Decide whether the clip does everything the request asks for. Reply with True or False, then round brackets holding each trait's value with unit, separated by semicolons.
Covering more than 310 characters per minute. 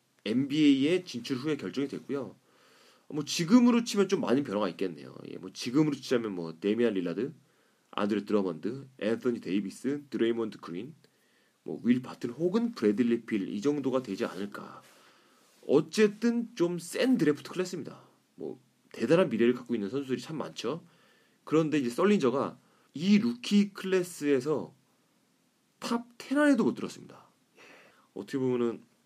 True (320 characters per minute)